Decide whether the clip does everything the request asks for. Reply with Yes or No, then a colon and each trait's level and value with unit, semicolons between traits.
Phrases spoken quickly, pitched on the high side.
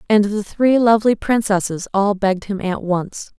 No: average, 175 wpm; high, 205 Hz